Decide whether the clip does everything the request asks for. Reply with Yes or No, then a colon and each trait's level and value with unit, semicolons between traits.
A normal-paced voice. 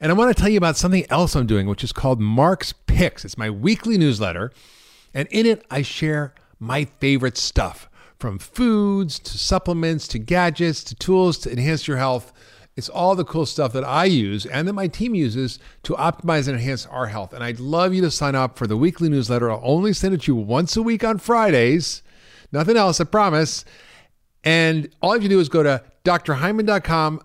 No: fast, 215 wpm